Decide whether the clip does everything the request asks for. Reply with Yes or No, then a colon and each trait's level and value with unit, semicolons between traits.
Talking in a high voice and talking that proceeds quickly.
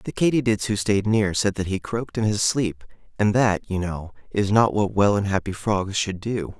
No: low, 100 Hz; fast, 225 wpm